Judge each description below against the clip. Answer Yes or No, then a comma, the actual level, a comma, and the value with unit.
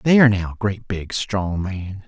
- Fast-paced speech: No, average, 175 wpm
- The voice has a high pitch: No, low, 100 Hz